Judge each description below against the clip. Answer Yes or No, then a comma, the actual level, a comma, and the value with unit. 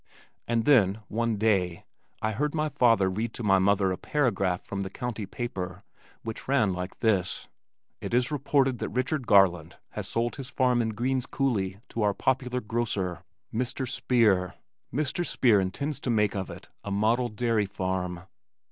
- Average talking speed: Yes, average, 165 wpm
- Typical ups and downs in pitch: Yes, average, 4.5 semitones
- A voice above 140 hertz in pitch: No, low, 110 Hz